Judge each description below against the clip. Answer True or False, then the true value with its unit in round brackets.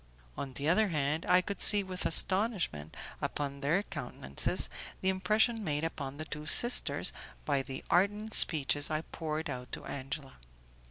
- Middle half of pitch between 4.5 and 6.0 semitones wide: True (5.2 semitones)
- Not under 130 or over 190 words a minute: True (155 wpm)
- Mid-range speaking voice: True (155 Hz)